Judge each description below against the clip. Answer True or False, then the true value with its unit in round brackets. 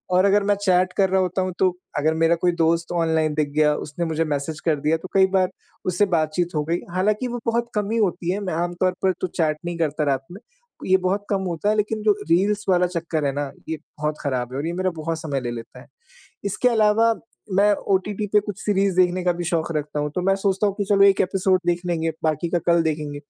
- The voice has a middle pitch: True (175 Hz)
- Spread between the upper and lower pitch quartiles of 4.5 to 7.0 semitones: False (3.7 semitones)